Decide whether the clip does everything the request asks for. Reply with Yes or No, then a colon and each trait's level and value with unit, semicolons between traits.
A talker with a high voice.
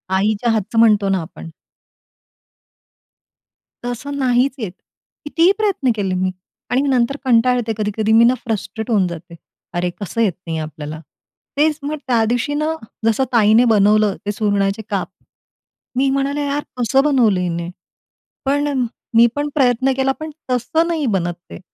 Yes: high, 230 Hz